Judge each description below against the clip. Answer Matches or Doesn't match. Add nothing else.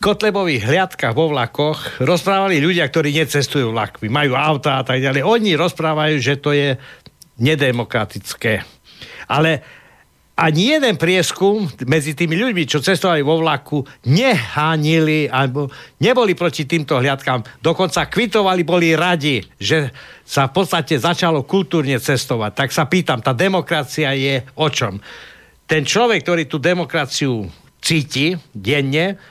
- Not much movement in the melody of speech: Doesn't match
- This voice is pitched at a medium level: Matches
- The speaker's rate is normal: Matches